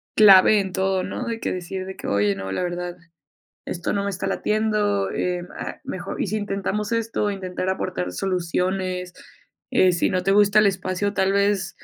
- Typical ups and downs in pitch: No, narrow, 2.0 semitones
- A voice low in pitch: No, high, 190 Hz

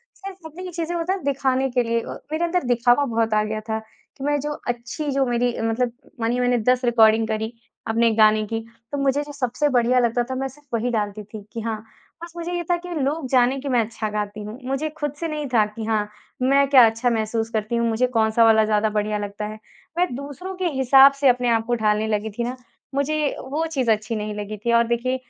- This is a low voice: No, high, 240 Hz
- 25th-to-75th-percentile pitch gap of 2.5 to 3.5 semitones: No, average, 4.0 semitones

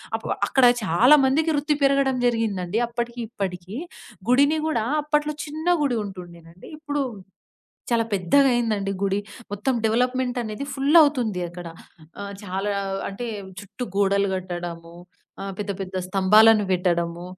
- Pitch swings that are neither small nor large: No, wide, 5.9 semitones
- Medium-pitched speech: No, high, 215 Hz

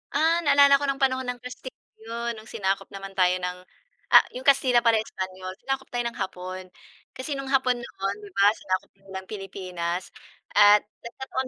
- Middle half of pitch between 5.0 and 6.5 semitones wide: Yes, wide, 5.5 semitones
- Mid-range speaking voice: No, high, 220 Hz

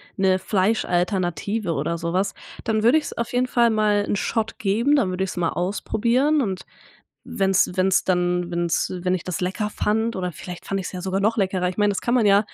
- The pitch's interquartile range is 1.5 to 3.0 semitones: No, average, 3.4 semitones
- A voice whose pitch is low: No, high, 195 Hz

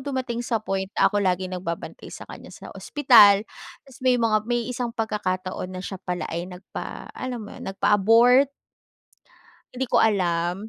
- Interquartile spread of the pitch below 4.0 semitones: No, average, 4.6 semitones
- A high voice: Yes, high, 210 Hz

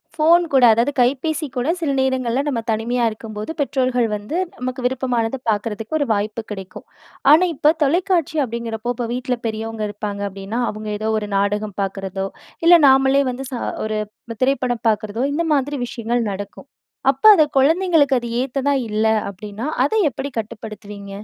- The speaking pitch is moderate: No, high, 240 Hz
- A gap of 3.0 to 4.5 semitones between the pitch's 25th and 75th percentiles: Yes, average, 4.2 semitones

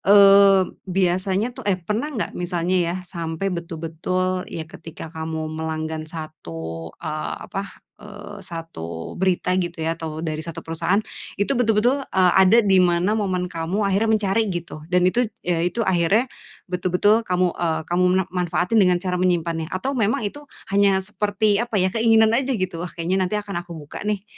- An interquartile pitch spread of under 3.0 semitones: No, average, 3.6 semitones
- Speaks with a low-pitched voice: No, medium, 185 Hz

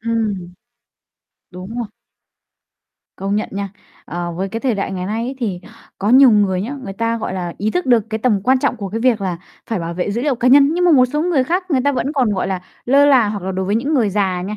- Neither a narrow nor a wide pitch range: Yes, average, 4.9 semitones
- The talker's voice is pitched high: Yes, high, 220 Hz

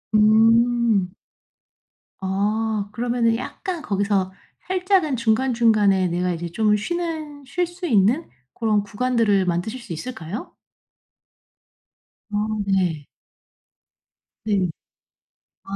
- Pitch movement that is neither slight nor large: Yes, average, 4.4 semitones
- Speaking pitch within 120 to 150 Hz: No, high, 220 Hz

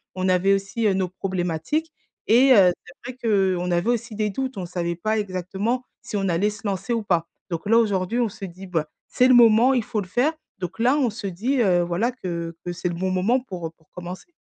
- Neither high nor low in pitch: No, high, 195 Hz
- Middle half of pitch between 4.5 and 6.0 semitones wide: Yes, average, 4.8 semitones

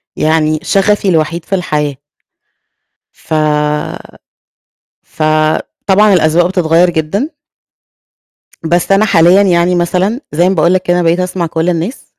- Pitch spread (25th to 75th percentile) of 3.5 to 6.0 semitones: No, average, 2.9 semitones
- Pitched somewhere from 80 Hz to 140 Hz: No, medium, 175 Hz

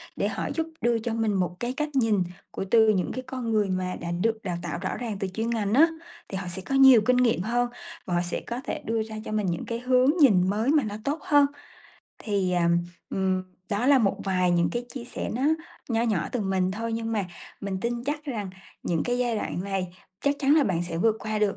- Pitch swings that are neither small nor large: Yes, average, 4.4 semitones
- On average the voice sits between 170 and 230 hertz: Yes, high, 220 Hz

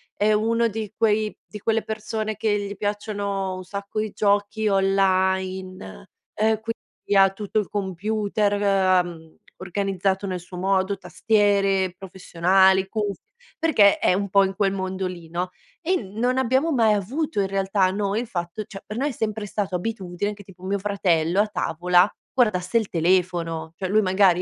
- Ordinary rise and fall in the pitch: No, narrow, 2.3 semitones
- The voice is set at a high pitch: Yes, high, 200 Hz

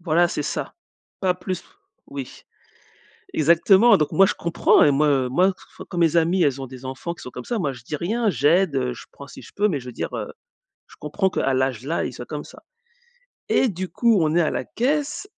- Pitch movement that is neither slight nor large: No, wide, 5.7 semitones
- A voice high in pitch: No, medium, 165 Hz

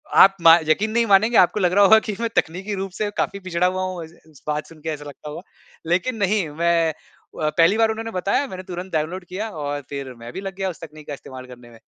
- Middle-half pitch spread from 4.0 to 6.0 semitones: Yes, average, 4.4 semitones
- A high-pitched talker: No, medium, 180 Hz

